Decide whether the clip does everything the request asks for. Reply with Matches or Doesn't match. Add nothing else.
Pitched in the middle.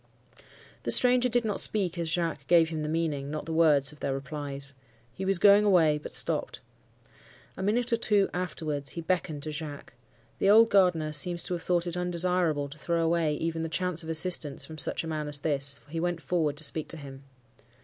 Matches